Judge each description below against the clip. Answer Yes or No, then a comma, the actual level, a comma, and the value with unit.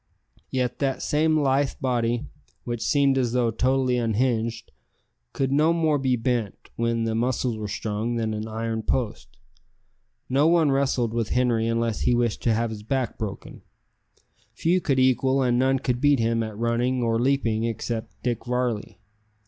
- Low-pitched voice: Yes, low, 120 Hz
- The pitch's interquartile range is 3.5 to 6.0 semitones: No, average, 2.7 semitones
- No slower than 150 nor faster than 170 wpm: Yes, average, 165 wpm